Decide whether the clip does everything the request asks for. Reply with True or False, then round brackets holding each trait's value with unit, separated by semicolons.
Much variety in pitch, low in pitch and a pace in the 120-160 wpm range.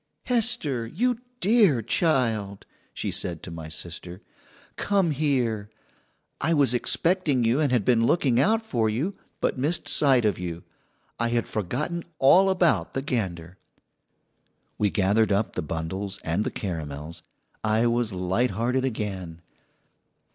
True (7.3 semitones; 115 Hz; 140 wpm)